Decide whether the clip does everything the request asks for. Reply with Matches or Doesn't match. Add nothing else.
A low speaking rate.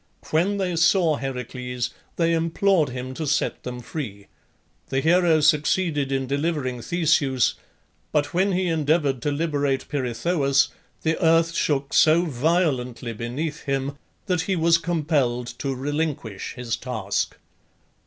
Matches